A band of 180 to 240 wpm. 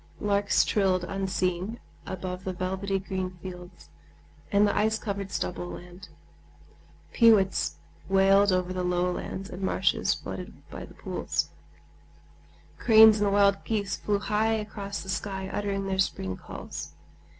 No: slow, 135 wpm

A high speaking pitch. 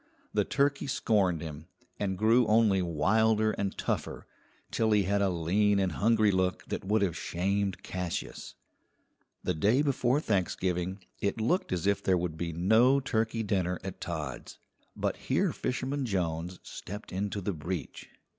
No: low, 100 Hz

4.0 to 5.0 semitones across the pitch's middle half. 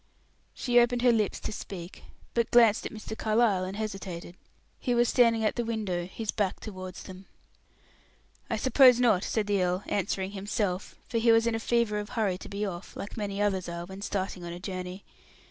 No: average, 3.5 semitones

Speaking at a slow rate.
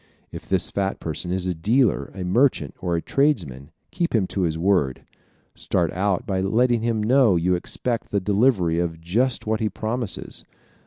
No: average, 175 wpm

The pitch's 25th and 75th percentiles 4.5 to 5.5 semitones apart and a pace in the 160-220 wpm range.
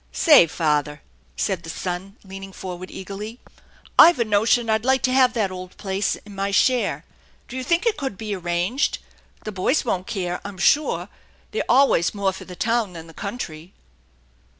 Yes: average, 4.9 semitones; average, 180 wpm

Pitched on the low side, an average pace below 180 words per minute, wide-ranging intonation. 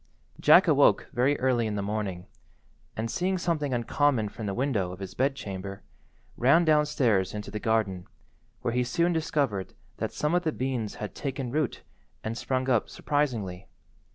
Yes: low, 120 Hz; average, 160 wpm; wide, 5.7 semitones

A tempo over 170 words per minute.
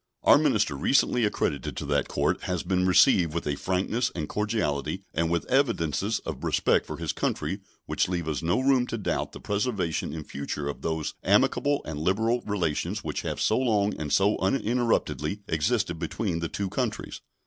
Yes: average, 180 wpm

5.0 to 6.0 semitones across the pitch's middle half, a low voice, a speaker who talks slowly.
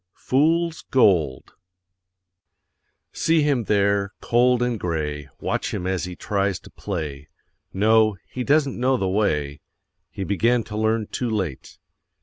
Yes: average, 5.3 semitones; low, 105 Hz; slow, 130 wpm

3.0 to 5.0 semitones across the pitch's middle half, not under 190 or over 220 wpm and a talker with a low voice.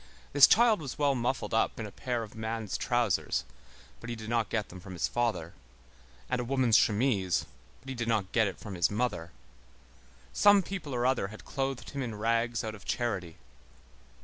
Yes: average, 3.5 semitones; average, 195 wpm; low, 115 Hz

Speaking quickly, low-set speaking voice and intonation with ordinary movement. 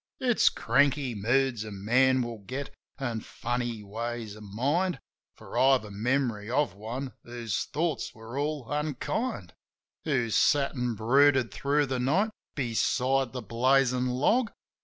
No: average, 140 wpm; low, 125 Hz; average, 3.5 semitones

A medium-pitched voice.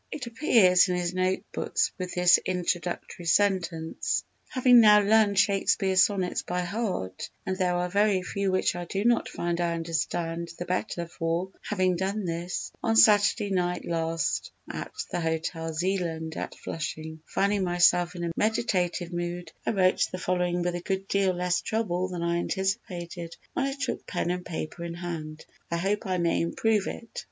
Yes: medium, 180 Hz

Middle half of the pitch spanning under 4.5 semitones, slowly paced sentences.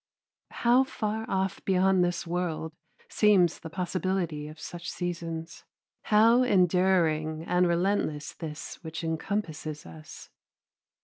Yes: average, 3.1 semitones; slow, 110 wpm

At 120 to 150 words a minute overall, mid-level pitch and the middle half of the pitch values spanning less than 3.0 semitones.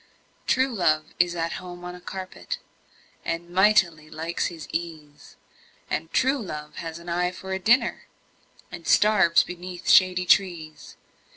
Yes: average, 145 wpm; medium, 175 Hz; narrow, 2.4 semitones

